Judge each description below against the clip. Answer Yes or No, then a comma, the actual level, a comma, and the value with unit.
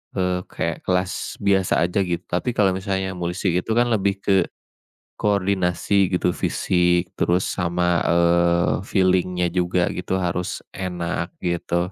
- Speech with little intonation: Yes, narrow, 1.6 semitones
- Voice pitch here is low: Yes, very low, 90 Hz